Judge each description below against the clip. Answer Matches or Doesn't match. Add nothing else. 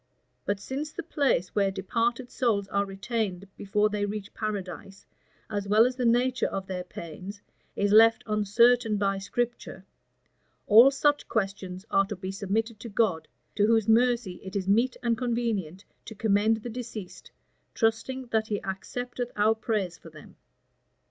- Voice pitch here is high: Matches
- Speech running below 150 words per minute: Doesn't match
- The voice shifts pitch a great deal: Doesn't match